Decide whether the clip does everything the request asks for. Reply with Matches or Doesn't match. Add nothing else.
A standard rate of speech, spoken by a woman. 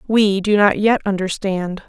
Matches